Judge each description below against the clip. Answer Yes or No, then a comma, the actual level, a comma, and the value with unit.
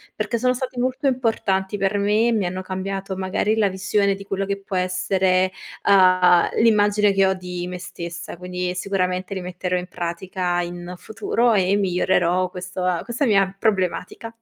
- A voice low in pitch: No, high, 190 Hz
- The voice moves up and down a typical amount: No, narrow, 2.2 semitones